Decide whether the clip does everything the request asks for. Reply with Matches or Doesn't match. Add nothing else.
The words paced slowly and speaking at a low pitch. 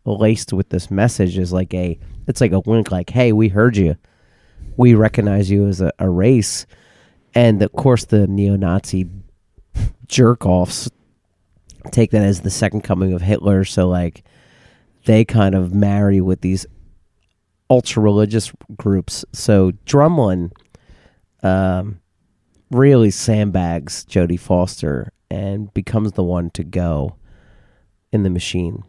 Matches